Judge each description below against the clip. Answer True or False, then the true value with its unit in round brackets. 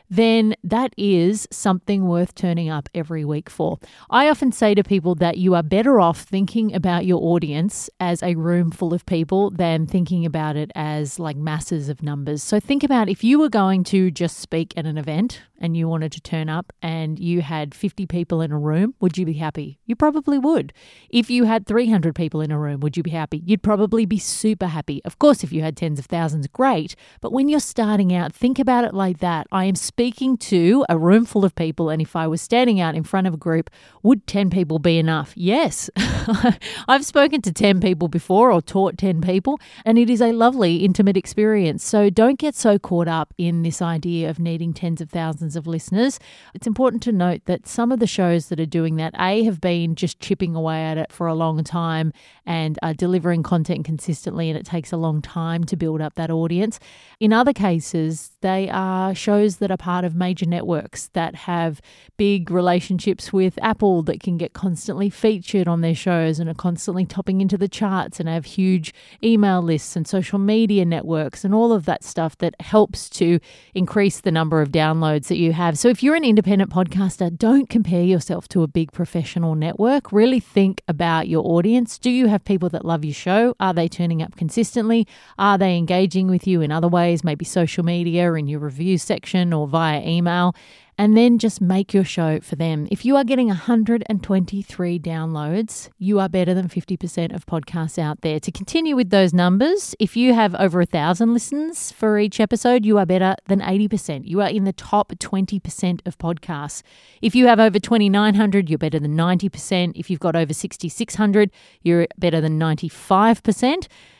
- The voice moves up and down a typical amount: True (4.0 semitones)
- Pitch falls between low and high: True (180 Hz)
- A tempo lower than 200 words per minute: False (205 wpm)